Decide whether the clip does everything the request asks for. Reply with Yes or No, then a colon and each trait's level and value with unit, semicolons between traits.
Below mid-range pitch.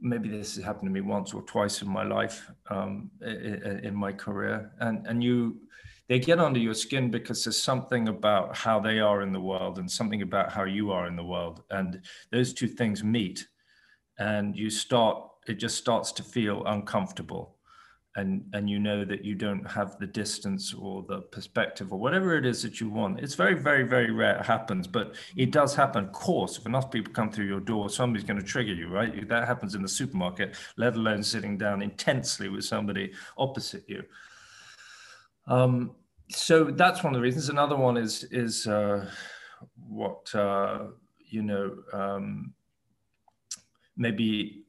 Yes: low, 110 Hz